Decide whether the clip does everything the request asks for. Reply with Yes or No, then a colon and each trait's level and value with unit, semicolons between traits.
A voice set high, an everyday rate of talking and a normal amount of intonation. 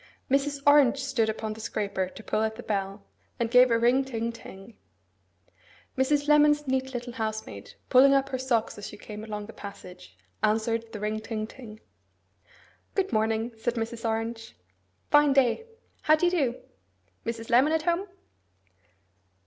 Yes: high, 230 Hz; average, 160 wpm; average, 3.8 semitones